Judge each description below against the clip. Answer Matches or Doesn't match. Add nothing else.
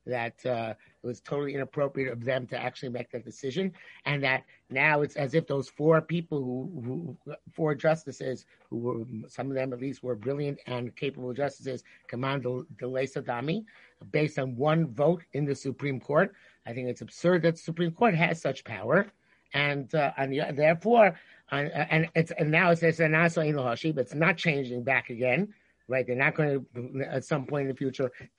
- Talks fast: Doesn't match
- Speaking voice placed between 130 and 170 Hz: Matches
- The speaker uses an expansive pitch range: Doesn't match